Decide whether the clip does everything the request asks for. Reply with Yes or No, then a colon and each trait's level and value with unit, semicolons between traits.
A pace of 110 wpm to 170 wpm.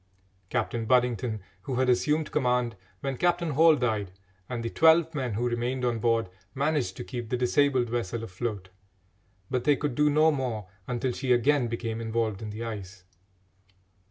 Yes: average, 165 wpm